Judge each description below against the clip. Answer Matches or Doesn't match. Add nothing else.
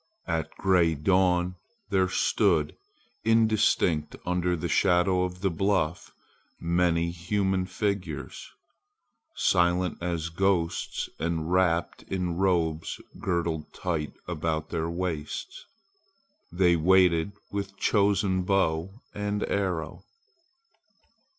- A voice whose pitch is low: Matches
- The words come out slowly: Matches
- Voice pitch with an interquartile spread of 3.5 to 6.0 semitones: Doesn't match